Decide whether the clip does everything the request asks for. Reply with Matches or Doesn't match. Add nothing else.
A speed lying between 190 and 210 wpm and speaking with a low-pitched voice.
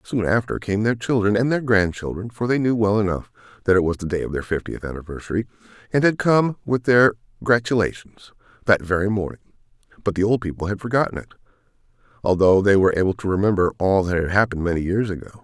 Matches